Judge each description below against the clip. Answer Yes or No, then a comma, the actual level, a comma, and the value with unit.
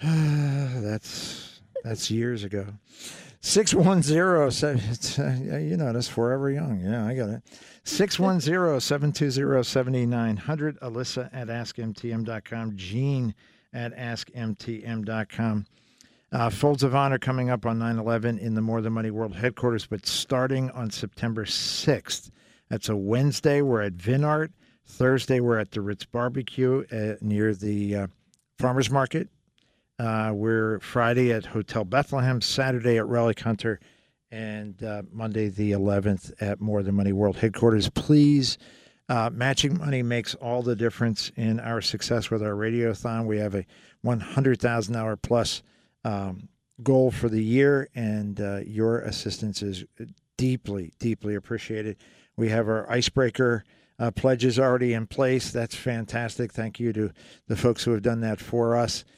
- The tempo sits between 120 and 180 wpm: Yes, slow, 135 wpm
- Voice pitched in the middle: No, low, 115 Hz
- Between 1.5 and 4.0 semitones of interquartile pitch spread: Yes, average, 3.0 semitones